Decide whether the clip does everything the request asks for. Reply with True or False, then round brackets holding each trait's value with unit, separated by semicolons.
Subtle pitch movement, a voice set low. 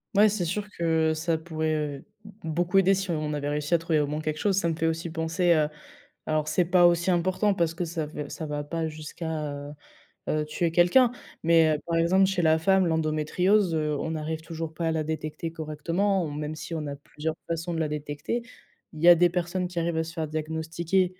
False (2.1 semitones; 160 Hz)